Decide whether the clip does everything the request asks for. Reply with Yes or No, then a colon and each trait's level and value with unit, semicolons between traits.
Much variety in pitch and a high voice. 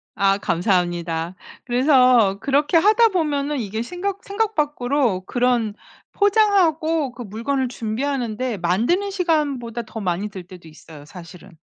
Yes: wide, 7.7 semitones; high, 245 Hz